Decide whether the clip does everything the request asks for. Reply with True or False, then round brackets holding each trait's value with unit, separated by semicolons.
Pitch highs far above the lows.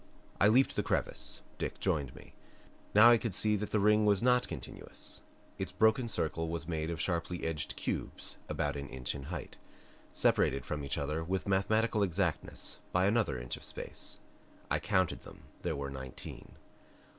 True (6.0 semitones)